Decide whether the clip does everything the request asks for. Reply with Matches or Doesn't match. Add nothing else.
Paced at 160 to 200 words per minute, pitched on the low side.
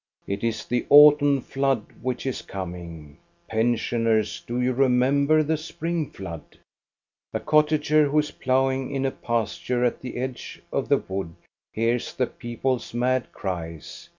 Doesn't match